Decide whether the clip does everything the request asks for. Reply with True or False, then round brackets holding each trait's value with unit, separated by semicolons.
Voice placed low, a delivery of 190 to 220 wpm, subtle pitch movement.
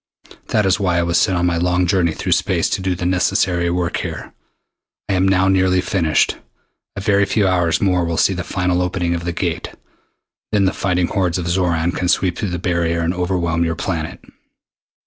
True (90 Hz; 205 wpm; 1.6 semitones)